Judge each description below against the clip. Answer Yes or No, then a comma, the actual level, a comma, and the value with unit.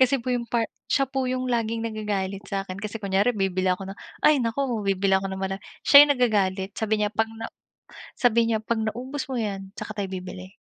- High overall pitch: Yes, high, 215 Hz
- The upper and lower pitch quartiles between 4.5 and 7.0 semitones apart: No, average, 3.4 semitones